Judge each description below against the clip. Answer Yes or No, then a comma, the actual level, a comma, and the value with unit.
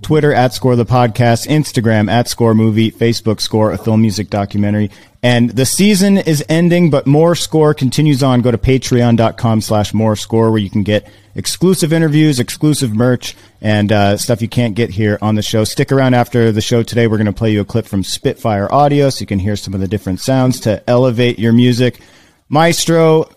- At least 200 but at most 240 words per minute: Yes, fast, 205 wpm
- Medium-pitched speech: No, low, 115 Hz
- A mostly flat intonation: No, average, 3.9 semitones